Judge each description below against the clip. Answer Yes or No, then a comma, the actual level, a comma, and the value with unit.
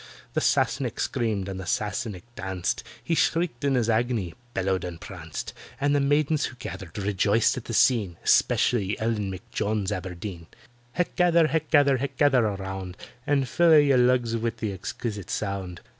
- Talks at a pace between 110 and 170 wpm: Yes, average, 160 wpm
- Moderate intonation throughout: No, wide, 5.9 semitones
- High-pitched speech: No, low, 110 Hz